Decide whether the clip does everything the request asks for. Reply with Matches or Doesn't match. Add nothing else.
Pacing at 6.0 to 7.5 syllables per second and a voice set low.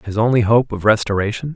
Matches